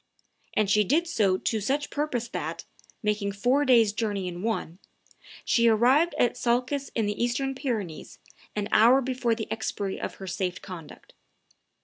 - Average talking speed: Yes, average, 155 wpm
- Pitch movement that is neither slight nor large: Yes, average, 4.2 semitones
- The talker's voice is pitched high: Yes, high, 225 Hz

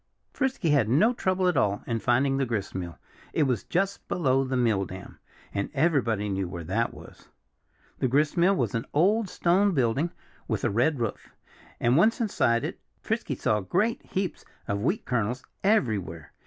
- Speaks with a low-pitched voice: Yes, low, 130 Hz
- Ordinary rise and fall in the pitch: No, wide, 8.6 semitones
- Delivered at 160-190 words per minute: Yes, average, 170 wpm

